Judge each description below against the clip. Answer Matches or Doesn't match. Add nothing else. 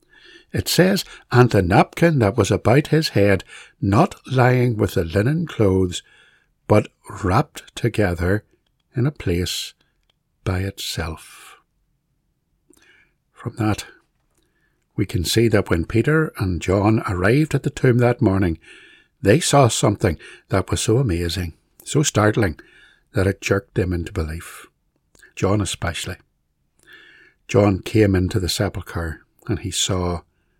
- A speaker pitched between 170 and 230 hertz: Doesn't match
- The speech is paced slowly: Matches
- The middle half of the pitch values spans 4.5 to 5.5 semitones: Matches